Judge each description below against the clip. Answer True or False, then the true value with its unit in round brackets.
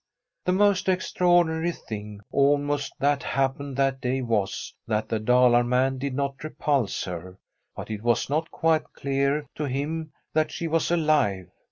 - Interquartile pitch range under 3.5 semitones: False (4.4 semitones)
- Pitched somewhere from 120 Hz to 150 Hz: True (140 Hz)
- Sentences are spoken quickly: False (155 wpm)